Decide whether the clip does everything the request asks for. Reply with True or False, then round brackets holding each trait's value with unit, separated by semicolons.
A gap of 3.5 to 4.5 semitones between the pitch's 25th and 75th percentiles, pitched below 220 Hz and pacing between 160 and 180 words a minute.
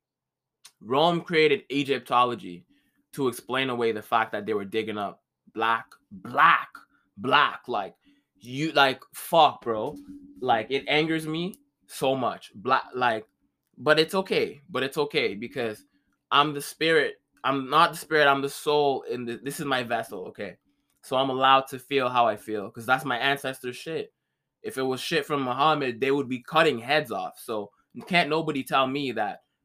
True (4.0 semitones; 140 Hz; 170 wpm)